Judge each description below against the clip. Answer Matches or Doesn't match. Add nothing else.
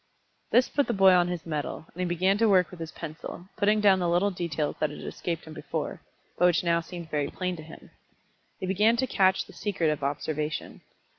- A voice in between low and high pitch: Matches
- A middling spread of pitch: Matches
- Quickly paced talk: Matches